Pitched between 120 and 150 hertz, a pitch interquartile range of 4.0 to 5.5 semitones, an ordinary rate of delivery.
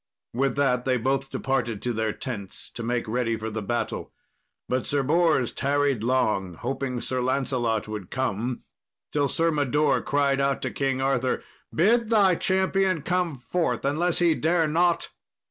Yes: low, 135 Hz; average, 4.4 semitones; average, 160 wpm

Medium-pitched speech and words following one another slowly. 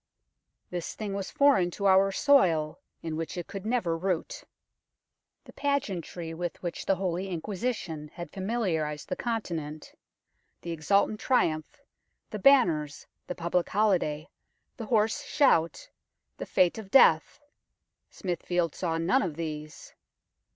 Yes: medium, 180 Hz; slow, 130 wpm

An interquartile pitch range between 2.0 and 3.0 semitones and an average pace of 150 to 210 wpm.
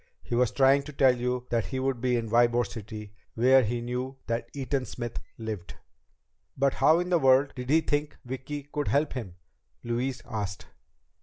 Yes: narrow, 2.5 semitones; average, 180 wpm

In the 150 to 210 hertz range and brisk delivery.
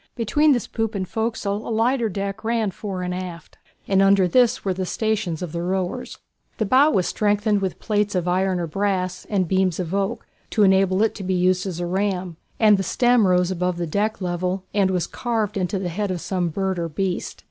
Yes: high, 190 Hz; fast, 215 wpm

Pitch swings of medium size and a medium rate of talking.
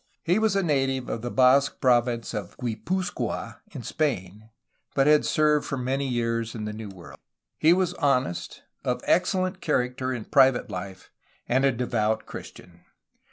Yes: average, 4.7 semitones; average, 160 wpm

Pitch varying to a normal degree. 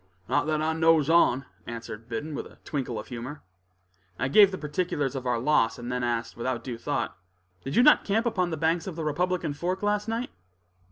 No: wide, 6.2 semitones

